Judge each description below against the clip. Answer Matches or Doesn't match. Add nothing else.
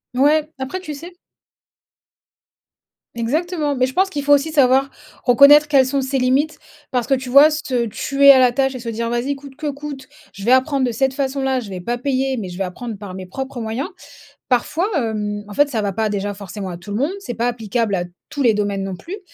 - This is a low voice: Doesn't match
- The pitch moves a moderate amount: Matches